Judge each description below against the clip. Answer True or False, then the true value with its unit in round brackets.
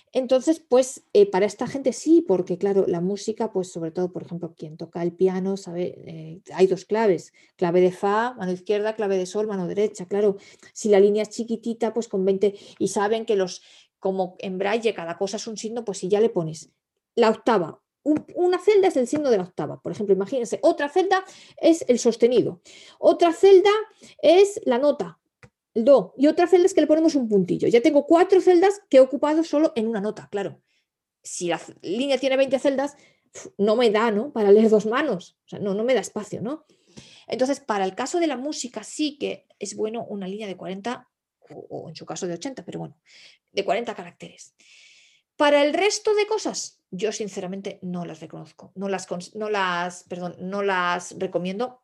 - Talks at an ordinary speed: False (200 wpm)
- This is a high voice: True (215 Hz)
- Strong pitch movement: True (6.7 semitones)